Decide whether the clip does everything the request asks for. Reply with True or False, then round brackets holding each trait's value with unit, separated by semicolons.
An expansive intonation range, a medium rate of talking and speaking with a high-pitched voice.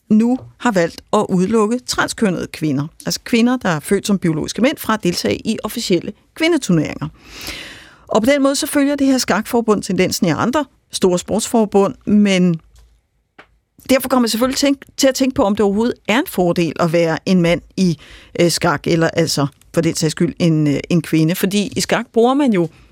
True (6.0 semitones; 185 wpm; 200 Hz)